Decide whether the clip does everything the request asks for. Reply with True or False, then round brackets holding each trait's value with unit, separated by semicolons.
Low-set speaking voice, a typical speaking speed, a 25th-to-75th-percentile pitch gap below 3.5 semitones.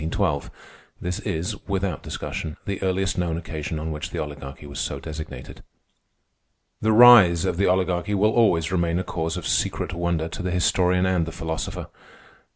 True (85 Hz; 165 wpm; 2.6 semitones)